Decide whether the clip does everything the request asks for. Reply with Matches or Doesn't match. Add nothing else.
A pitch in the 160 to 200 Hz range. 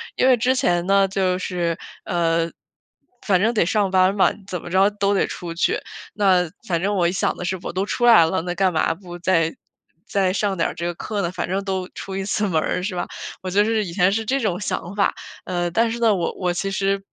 Matches